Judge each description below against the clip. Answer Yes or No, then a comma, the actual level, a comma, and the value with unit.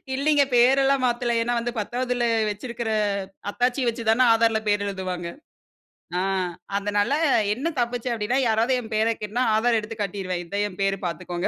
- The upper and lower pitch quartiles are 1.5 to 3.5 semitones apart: Yes, average, 3.1 semitones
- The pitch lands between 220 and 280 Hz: Yes, high, 225 Hz